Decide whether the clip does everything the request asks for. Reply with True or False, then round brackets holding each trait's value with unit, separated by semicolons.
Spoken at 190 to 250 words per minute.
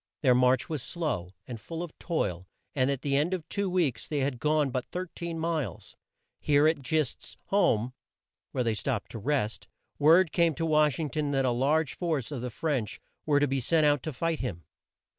True (200 wpm)